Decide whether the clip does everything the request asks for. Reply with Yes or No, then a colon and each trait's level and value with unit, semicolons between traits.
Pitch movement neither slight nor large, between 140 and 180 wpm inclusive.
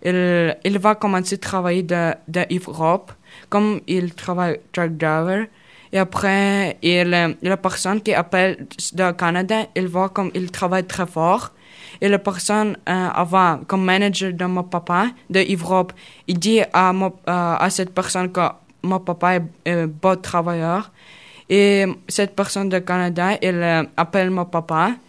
No: narrow, 1.7 semitones; average, 150 wpm